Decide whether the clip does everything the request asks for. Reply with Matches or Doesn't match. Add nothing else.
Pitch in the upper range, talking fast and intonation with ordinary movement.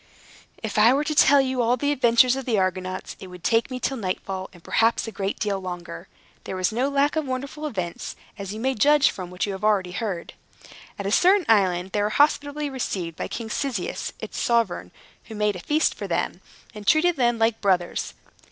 Doesn't match